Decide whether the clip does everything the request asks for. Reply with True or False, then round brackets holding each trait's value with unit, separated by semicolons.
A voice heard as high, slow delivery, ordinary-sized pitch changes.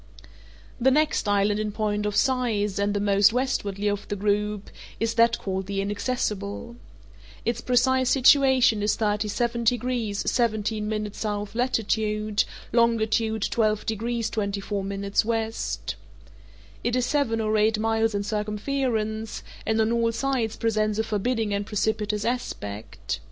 False (220 Hz; 130 wpm; 2.2 semitones)